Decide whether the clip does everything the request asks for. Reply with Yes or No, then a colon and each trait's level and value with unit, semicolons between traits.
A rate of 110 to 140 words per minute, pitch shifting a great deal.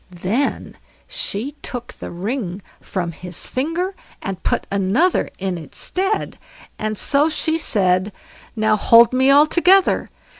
Yes: slow, 135 wpm; wide, 7.8 semitones